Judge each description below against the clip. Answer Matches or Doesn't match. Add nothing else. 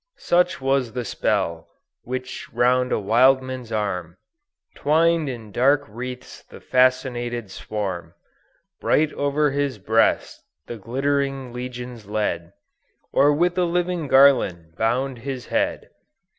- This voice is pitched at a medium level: Doesn't match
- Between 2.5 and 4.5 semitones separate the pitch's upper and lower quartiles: Matches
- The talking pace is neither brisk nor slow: Doesn't match